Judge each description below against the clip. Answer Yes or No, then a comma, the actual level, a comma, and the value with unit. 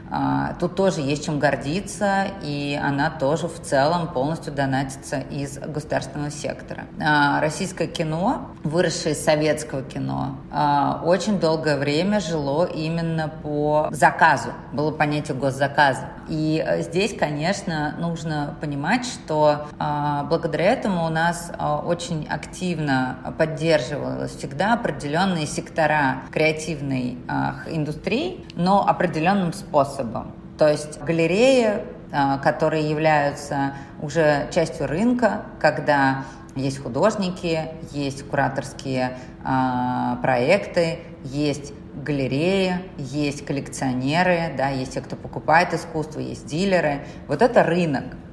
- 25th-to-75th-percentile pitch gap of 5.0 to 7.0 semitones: No, average, 3.0 semitones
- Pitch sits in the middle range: Yes, medium, 155 Hz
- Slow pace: Yes, slow, 100 wpm